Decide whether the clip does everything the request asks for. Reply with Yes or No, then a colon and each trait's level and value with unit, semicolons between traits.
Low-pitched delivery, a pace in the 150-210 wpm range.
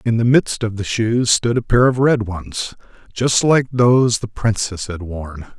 Yes: low, 110 Hz; fast, 205 wpm